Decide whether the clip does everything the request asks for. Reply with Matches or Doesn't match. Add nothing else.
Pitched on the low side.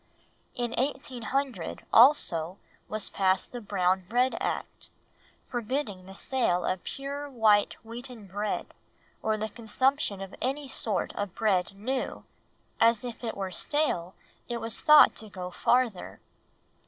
Doesn't match